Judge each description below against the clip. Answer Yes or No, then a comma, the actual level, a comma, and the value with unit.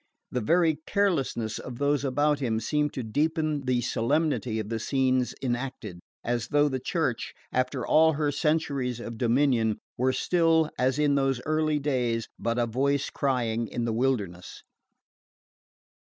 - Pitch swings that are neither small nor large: Yes, average, 3.9 semitones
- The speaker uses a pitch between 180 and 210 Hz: No, low, 130 Hz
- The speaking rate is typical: Yes, average, 150 wpm